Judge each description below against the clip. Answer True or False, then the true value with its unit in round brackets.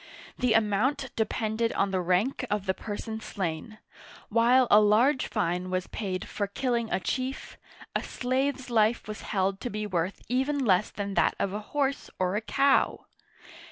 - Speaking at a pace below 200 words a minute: True (165 wpm)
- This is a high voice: True (215 Hz)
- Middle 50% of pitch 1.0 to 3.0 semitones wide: False (4.3 semitones)